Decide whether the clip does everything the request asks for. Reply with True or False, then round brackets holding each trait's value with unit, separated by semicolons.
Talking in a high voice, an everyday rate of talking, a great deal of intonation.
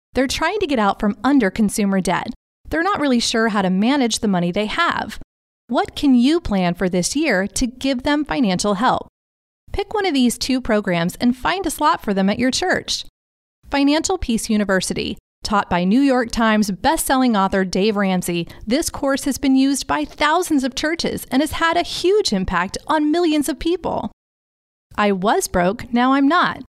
True (255 Hz; 190 wpm; 6.7 semitones)